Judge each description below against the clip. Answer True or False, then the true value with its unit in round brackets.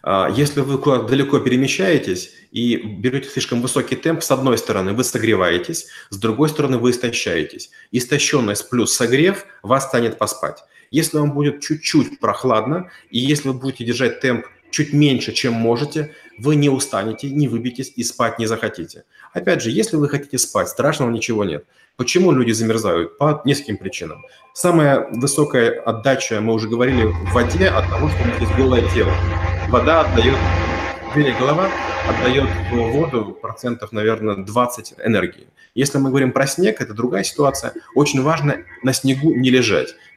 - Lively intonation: False (4.3 semitones)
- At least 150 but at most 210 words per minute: True (155 wpm)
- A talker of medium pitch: False (125 Hz)